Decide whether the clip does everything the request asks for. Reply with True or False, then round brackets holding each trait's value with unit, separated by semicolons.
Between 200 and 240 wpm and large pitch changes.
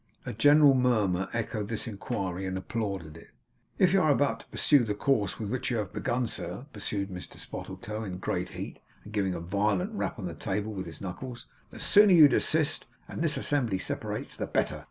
True (205 wpm; 5.7 semitones)